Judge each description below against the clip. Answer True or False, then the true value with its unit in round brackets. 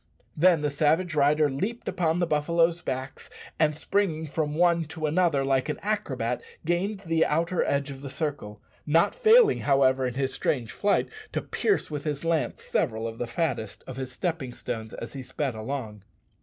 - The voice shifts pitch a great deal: False (4.2 semitones)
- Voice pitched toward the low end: False (150 Hz)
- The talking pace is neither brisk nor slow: True (180 wpm)